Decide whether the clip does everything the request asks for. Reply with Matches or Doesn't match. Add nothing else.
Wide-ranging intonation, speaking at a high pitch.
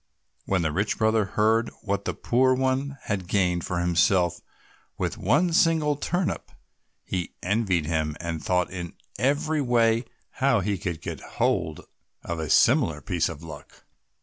Doesn't match